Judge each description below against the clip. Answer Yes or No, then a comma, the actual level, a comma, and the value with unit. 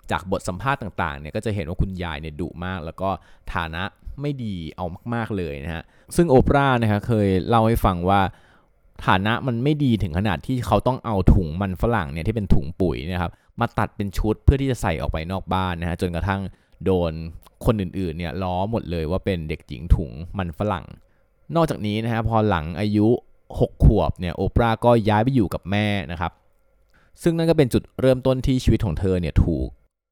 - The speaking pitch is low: Yes, very low, 95 Hz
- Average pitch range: Yes, average, 4.5 semitones